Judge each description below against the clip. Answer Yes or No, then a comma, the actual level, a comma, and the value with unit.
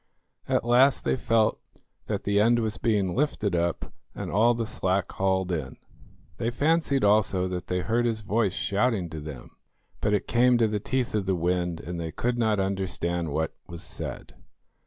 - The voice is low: Yes, low, 100 Hz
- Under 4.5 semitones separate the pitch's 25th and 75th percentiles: No, average, 4.8 semitones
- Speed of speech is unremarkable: Yes, average, 180 wpm